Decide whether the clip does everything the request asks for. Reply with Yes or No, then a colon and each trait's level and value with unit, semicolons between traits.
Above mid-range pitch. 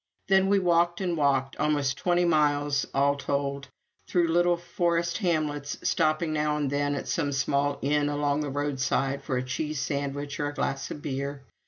No: medium, 145 Hz